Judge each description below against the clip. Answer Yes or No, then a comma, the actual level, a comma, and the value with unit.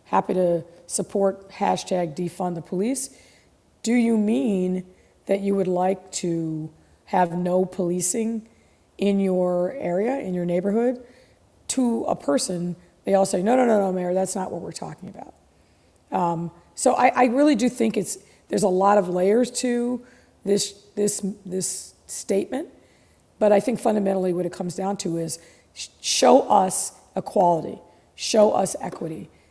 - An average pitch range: Yes, average, 3.7 semitones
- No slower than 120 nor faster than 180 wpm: Yes, average, 155 wpm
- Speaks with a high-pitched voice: Yes, high, 195 Hz